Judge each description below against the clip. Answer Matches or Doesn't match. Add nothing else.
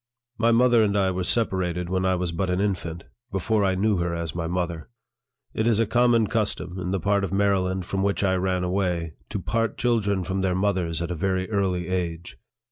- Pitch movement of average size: Doesn't match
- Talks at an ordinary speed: Doesn't match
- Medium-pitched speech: Doesn't match